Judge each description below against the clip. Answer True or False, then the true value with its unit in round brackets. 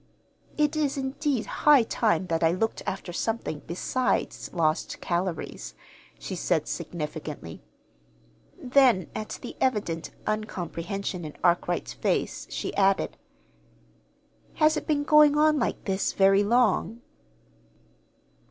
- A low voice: False (200 Hz)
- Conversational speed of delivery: False (115 wpm)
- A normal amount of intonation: False (7.3 semitones)